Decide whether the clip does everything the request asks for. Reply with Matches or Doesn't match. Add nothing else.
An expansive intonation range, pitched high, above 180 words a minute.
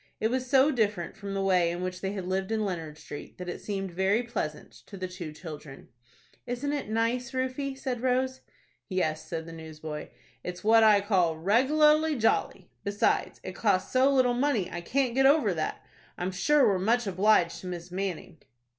Matches